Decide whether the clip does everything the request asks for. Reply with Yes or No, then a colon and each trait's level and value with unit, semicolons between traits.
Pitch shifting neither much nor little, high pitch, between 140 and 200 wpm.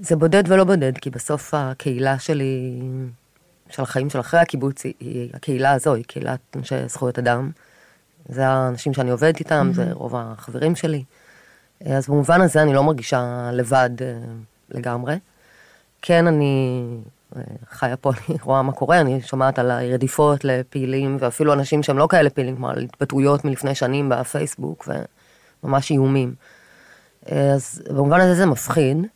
No: average, 3.3 semitones; low, 135 Hz; average, 145 wpm